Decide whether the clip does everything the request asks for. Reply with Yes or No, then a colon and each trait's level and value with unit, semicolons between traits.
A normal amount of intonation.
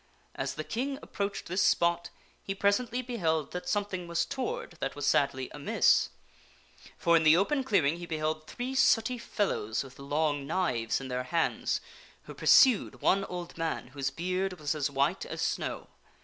No: wide, 5.7 semitones